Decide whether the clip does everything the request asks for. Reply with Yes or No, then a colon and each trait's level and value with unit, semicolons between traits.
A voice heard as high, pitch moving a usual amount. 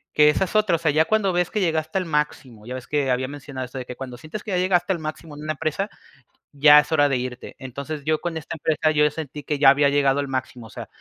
No: medium, 150 Hz; average, 3.0 semitones